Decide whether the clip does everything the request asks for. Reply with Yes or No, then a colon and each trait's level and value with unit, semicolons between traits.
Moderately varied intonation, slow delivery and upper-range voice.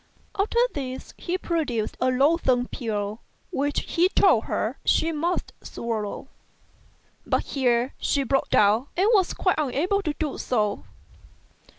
No: wide, 5.8 semitones; slow, 130 wpm; very high, 275 Hz